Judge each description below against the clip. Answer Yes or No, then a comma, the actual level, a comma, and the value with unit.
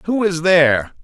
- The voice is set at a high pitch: No, medium, 165 Hz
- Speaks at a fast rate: No, average, 175 wpm